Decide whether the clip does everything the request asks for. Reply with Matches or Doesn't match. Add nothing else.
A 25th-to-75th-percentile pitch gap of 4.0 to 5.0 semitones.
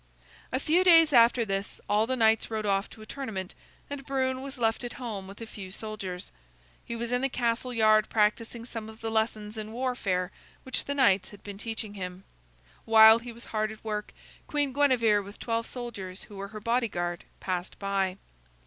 Doesn't match